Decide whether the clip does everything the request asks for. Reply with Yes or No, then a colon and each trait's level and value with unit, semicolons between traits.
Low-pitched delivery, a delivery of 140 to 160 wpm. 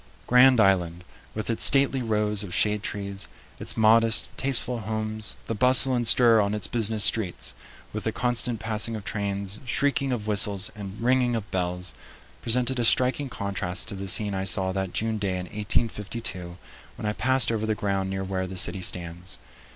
No: low, 105 Hz; average, 180 wpm